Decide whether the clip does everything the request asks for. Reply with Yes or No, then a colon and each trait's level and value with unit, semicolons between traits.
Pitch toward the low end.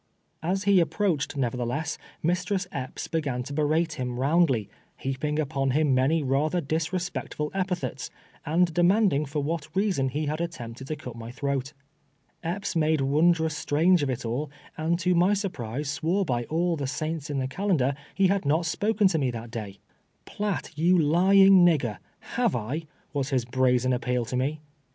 No: medium, 155 Hz